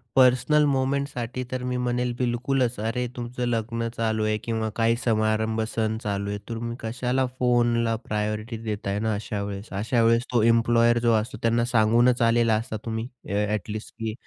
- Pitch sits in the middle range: No, low, 115 Hz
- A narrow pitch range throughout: Yes, narrow, 2.1 semitones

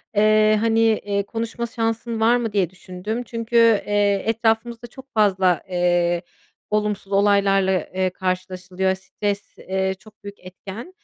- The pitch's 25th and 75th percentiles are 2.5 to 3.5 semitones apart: Yes, average, 3.1 semitones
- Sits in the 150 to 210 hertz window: Yes, high, 205 Hz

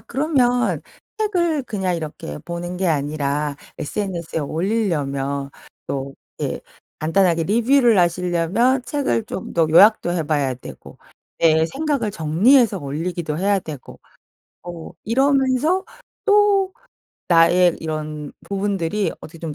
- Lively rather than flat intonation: Yes, wide, 7.3 semitones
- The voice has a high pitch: No, medium, 180 Hz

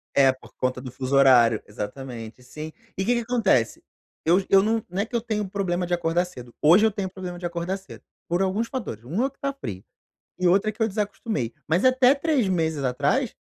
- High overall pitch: No, medium, 180 Hz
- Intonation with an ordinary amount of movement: No, wide, 8.1 semitones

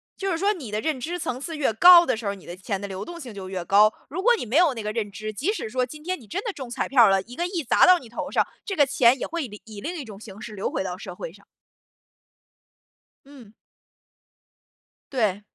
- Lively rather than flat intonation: Yes, wide, 7.9 semitones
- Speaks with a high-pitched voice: Yes, high, 240 Hz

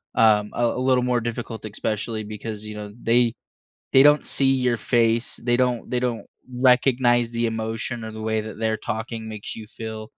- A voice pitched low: Yes, low, 115 Hz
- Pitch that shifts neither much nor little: No, narrow, 1.9 semitones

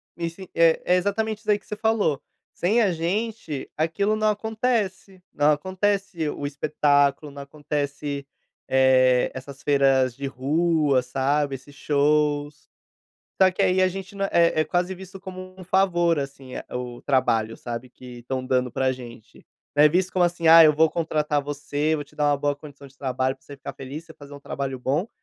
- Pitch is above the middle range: No, medium, 150 Hz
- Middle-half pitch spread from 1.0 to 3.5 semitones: No, average, 4.9 semitones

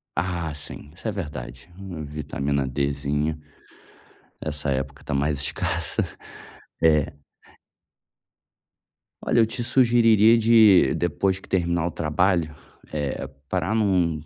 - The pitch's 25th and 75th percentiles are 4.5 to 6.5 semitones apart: Yes, average, 5.0 semitones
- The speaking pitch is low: Yes, very low, 80 Hz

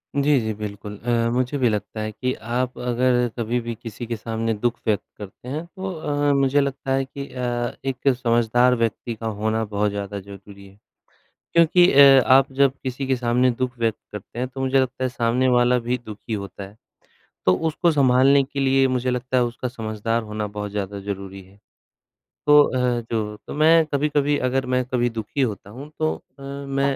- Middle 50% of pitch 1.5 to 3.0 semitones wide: No, average, 3.6 semitones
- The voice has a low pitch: Yes, low, 125 Hz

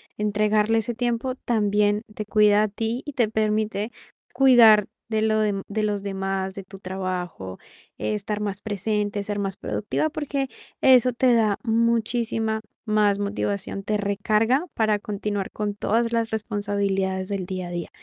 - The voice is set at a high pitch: Yes, high, 210 Hz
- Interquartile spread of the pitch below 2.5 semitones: Yes, narrow, 1.9 semitones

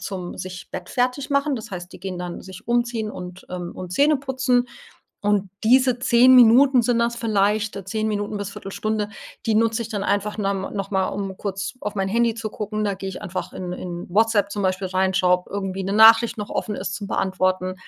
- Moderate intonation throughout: Yes, average, 3.3 semitones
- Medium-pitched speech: No, high, 205 Hz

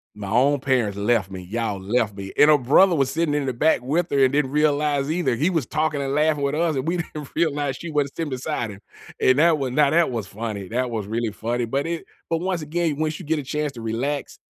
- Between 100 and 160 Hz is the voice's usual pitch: Yes, medium, 140 Hz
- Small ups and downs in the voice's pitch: No, average, 4.6 semitones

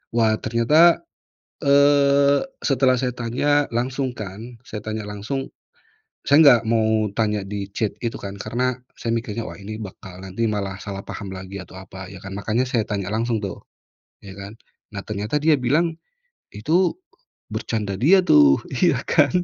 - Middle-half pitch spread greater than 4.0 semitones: Yes, average, 4.5 semitones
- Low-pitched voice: Yes, low, 110 Hz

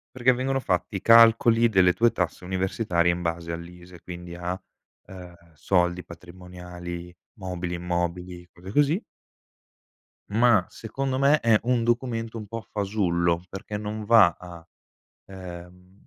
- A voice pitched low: Yes, very low, 90 Hz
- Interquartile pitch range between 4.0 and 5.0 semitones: Yes, average, 4.5 semitones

